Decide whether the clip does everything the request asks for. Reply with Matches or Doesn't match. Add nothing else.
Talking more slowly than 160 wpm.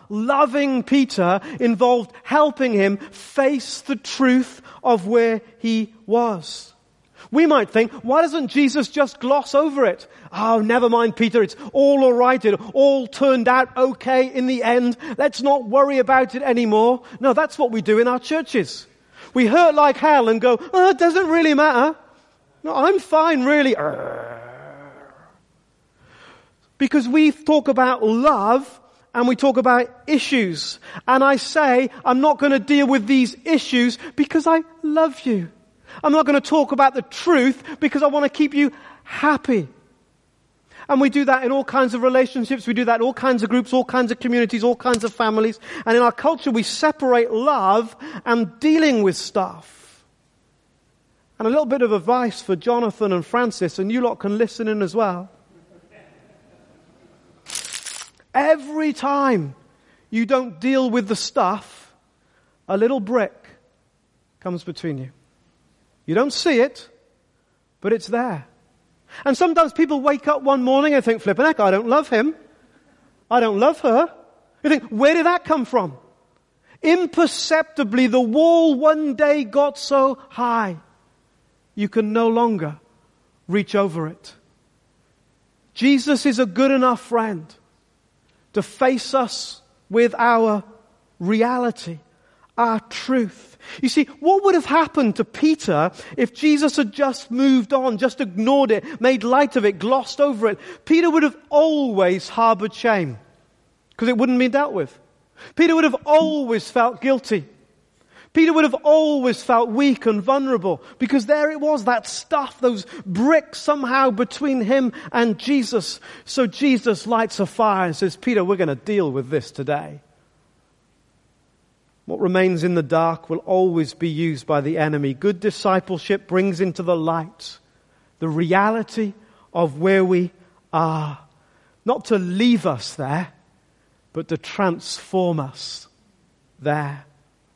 Matches